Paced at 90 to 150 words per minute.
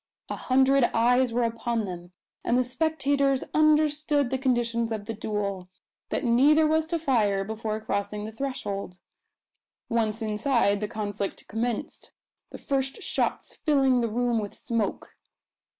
Yes: average, 140 wpm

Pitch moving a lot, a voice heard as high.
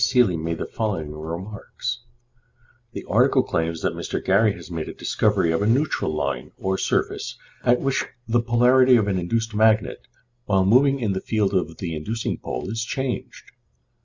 No: wide, 5.9 semitones; low, 105 Hz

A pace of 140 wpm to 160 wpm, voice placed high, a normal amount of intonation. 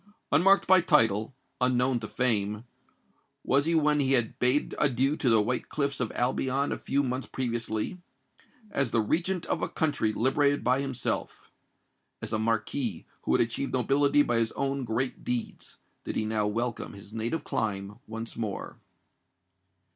No: average, 155 wpm; low, 125 Hz; average, 3.8 semitones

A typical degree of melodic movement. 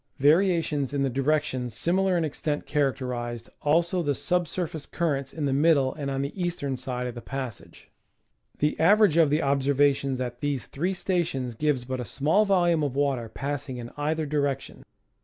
Yes: average, 3.5 semitones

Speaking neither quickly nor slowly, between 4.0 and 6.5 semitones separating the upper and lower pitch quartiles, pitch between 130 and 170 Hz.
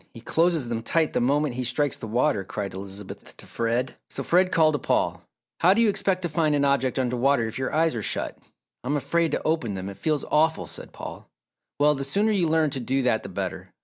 No: fast, 235 wpm; average, 5.0 semitones; medium, 140 Hz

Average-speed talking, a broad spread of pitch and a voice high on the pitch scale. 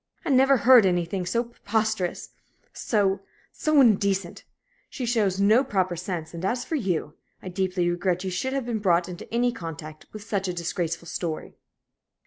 No: average, 165 wpm; average, 4.8 semitones; high, 195 Hz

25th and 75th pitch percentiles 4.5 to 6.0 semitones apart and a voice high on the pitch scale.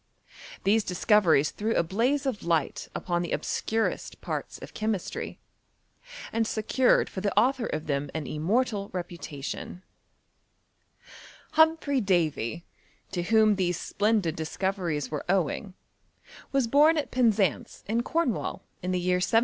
Yes: average, 4.9 semitones; high, 195 Hz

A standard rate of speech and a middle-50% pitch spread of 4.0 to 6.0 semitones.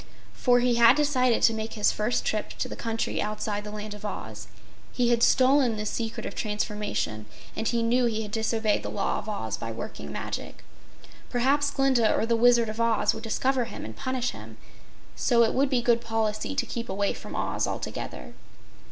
No: average, 195 wpm; narrow, 2.5 semitones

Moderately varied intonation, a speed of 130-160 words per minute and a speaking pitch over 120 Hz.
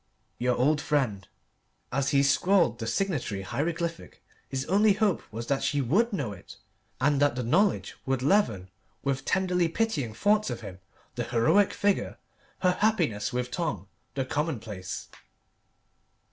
No: wide, 7.4 semitones; average, 145 wpm; medium, 140 Hz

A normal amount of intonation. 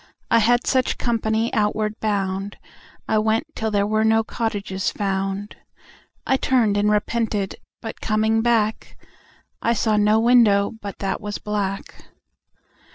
No: narrow, 1.6 semitones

